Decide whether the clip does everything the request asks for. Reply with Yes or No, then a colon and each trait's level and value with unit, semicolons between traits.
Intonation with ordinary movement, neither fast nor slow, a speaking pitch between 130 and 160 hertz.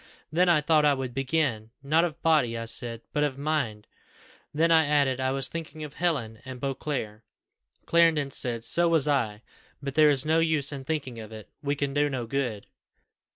Yes: average, 4.1 semitones; average, 195 wpm; medium, 140 Hz